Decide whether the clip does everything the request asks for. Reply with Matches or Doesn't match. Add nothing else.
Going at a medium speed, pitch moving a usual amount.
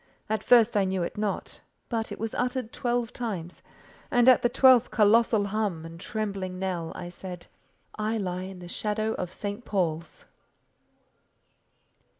Matches